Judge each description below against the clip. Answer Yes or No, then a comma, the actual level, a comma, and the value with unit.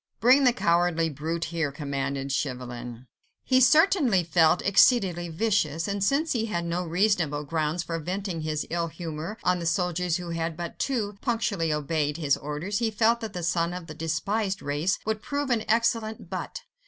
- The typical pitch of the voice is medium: Yes, medium, 175 Hz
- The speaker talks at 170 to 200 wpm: Yes, average, 175 wpm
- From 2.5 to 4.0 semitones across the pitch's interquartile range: No, average, 5.2 semitones